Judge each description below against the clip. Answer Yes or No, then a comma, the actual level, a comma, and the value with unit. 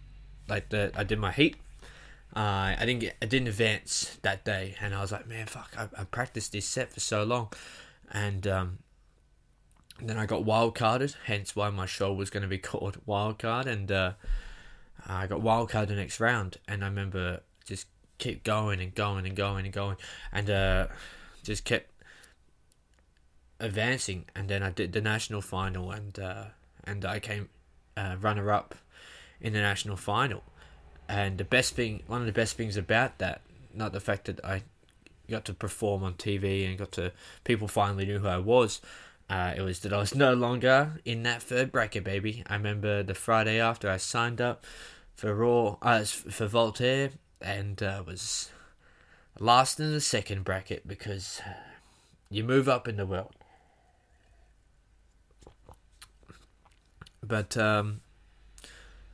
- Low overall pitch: Yes, low, 100 Hz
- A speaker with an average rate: Yes, average, 165 wpm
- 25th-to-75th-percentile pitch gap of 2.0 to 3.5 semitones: Yes, average, 2.8 semitones